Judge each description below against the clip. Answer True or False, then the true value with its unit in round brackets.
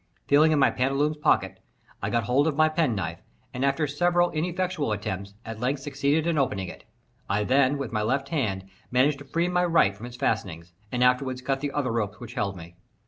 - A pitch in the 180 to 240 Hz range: False (135 Hz)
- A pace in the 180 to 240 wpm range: True (205 wpm)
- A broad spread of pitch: True (5.7 semitones)